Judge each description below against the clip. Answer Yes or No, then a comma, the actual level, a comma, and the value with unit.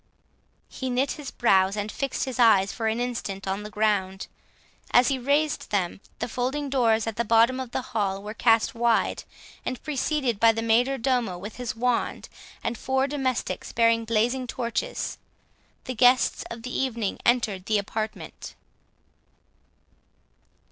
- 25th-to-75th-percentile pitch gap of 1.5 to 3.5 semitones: Yes, average, 3.0 semitones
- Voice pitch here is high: Yes, high, 230 Hz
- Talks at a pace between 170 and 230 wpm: No, average, 155 wpm